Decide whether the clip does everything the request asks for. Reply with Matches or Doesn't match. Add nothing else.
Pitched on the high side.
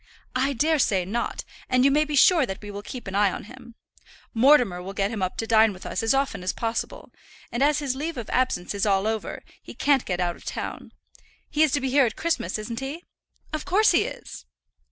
Matches